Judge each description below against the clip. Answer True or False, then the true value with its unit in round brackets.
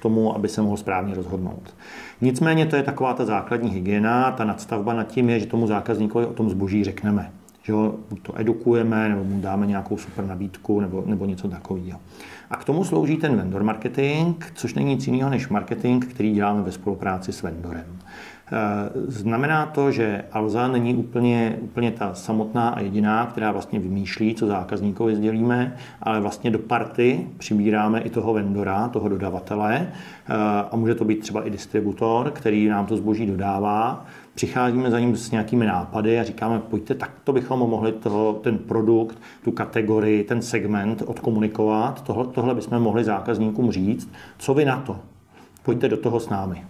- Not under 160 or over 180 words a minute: True (170 wpm)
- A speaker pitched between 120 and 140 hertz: False (110 Hz)